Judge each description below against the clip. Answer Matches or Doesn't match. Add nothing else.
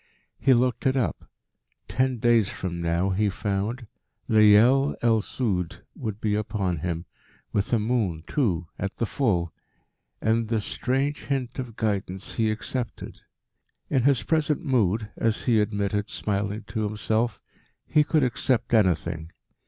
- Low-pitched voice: Matches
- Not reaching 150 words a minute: Matches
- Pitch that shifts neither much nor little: Matches